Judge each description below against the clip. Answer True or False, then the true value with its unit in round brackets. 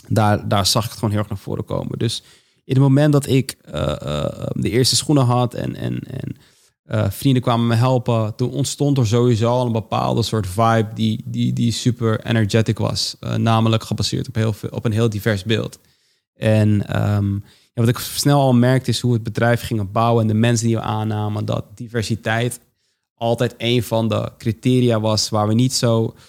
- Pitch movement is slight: True (2.0 semitones)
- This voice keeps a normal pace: False (205 wpm)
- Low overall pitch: True (115 Hz)